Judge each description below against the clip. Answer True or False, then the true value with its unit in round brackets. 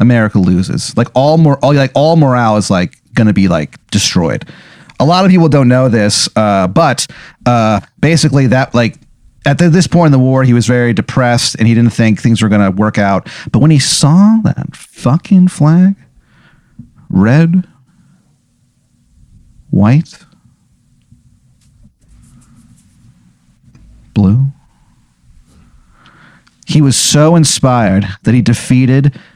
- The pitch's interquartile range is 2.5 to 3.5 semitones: False (4.9 semitones)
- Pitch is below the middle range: True (125 Hz)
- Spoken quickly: False (135 wpm)